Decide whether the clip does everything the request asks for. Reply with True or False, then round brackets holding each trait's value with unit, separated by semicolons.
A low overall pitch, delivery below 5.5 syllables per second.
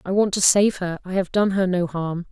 False (185 Hz; 5.1 syllables/s)